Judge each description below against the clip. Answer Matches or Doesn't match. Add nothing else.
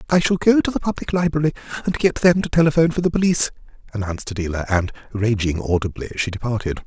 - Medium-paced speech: Matches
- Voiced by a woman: Doesn't match